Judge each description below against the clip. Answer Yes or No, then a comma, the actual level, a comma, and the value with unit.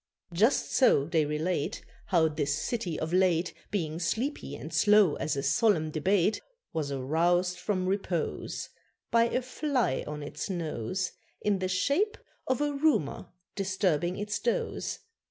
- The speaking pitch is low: No, medium, 180 Hz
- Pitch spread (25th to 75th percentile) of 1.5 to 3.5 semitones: No, average, 5.1 semitones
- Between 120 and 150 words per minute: Yes, average, 140 wpm